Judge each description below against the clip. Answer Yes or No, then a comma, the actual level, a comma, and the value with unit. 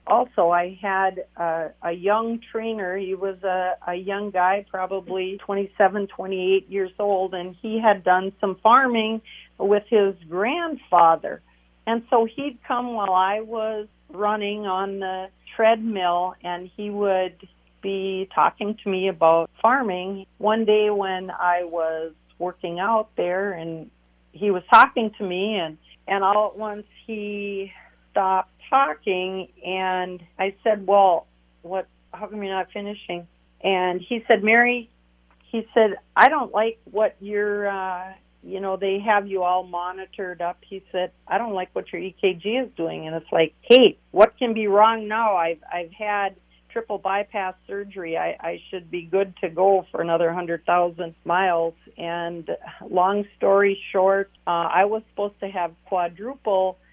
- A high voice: Yes, high, 195 Hz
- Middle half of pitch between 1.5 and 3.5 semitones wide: Yes, narrow, 2.6 semitones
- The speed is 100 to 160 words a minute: Yes, average, 155 wpm